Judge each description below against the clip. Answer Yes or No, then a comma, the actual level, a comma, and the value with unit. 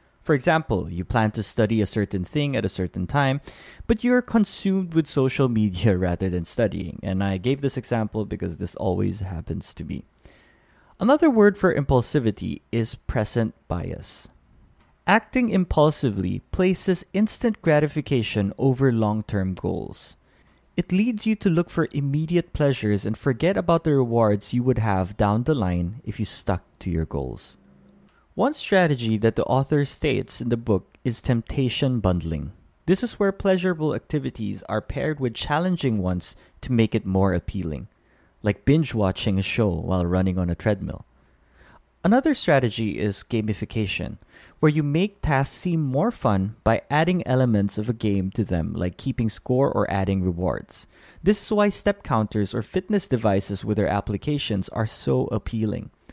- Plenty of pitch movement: Yes, wide, 7.6 semitones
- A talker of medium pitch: No, low, 115 Hz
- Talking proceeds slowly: No, average, 160 wpm